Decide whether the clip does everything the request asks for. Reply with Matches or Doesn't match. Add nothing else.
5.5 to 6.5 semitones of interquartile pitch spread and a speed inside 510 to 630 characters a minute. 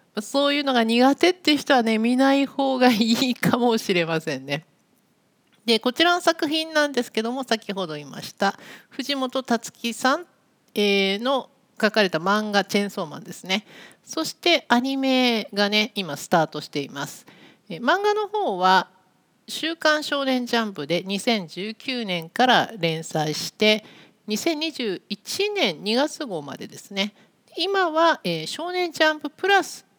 Doesn't match